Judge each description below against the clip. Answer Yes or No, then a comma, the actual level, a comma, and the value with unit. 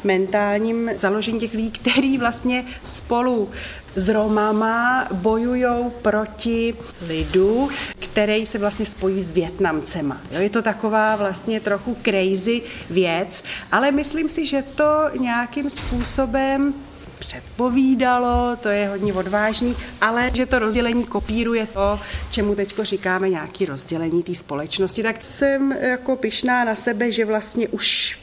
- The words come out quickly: No, average, 130 wpm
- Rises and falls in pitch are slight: No, average, 3.5 semitones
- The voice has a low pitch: No, high, 220 Hz